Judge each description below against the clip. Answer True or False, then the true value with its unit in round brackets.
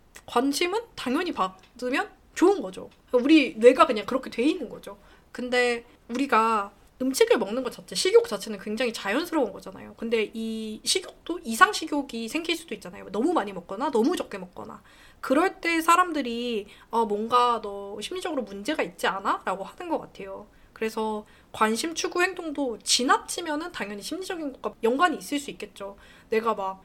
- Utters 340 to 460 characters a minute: True (350 characters per minute)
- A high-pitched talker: True (250 Hz)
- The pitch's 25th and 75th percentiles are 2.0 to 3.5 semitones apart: False (6.8 semitones)